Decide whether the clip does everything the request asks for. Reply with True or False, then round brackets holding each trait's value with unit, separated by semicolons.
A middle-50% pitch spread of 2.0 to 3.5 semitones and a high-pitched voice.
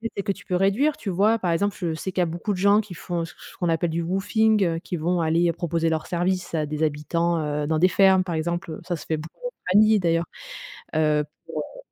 False (3.0 semitones; 175 Hz)